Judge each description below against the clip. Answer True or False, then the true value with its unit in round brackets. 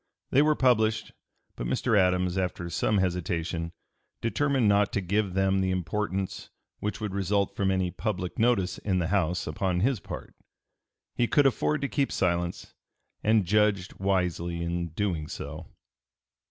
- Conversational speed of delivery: True (150 wpm)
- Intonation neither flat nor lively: True (3.1 semitones)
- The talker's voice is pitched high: False (95 Hz)